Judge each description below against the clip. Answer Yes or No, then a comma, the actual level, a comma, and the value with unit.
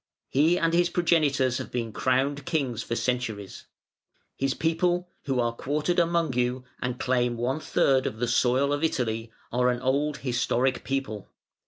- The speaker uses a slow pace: No, average, 160 wpm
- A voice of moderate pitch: No, low, 130 Hz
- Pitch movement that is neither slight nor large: Yes, average, 3.7 semitones